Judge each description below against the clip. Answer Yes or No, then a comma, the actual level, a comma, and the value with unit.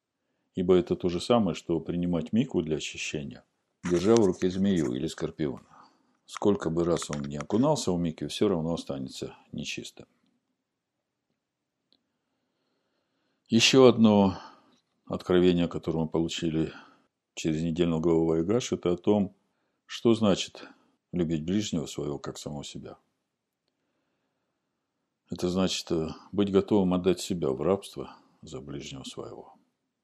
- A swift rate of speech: No, average, 120 wpm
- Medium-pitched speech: No, very low, 85 Hz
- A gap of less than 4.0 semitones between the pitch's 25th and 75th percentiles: Yes, average, 3.3 semitones